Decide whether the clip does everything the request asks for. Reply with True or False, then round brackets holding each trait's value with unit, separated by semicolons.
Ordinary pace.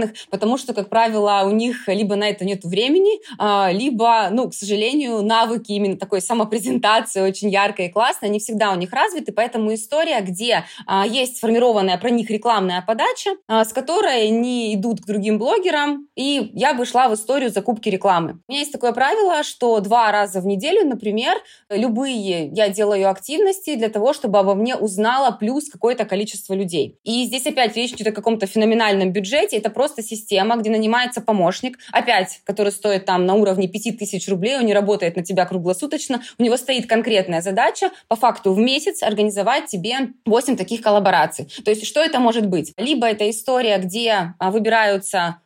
False (175 wpm)